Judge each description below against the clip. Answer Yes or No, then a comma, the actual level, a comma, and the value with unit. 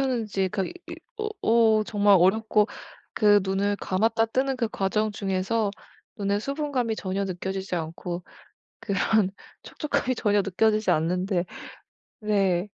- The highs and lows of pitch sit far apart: No, average, 2.7 semitones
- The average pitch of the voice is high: Yes, high, 205 Hz